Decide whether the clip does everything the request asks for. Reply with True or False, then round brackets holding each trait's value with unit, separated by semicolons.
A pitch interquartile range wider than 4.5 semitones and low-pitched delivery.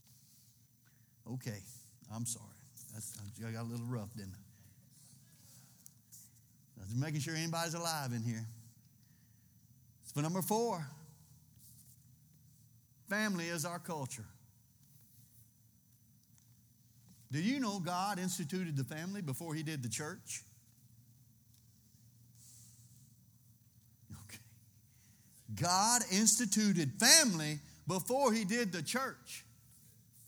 True (4.9 semitones; 125 Hz)